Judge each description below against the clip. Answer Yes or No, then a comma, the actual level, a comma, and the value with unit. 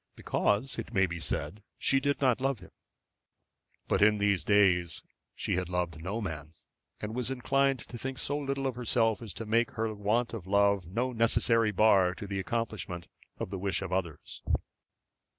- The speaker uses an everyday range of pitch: Yes, average, 4.2 semitones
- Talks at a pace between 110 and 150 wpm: No, average, 180 wpm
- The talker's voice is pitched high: No, low, 105 Hz